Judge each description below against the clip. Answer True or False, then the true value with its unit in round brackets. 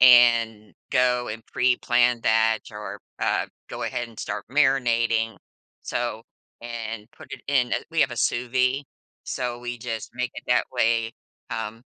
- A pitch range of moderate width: False (1.7 semitones)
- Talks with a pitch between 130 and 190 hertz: False (120 Hz)